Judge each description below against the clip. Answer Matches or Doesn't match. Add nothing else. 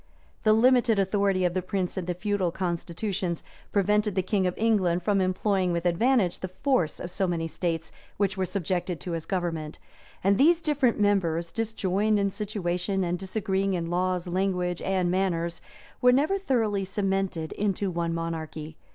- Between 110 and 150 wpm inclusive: Doesn't match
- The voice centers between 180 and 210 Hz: Matches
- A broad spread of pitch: Doesn't match